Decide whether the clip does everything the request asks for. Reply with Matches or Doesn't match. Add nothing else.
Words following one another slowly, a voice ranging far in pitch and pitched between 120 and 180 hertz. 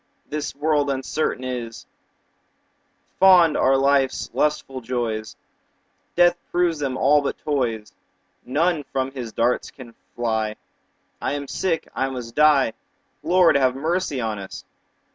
Doesn't match